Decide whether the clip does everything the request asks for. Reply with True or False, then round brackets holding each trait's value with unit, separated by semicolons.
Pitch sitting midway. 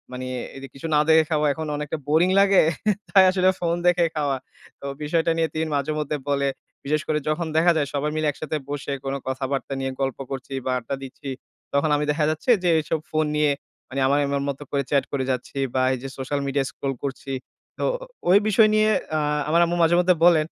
True (150 Hz)